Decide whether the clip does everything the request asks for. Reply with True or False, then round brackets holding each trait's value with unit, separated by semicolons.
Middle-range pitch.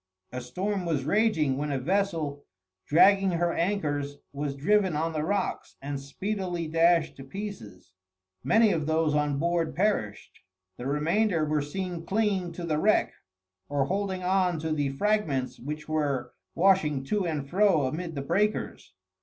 True (165 Hz)